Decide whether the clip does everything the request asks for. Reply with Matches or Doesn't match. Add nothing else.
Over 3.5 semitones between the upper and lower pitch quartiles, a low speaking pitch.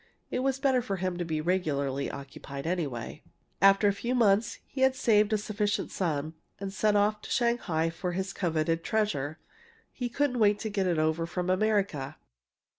Doesn't match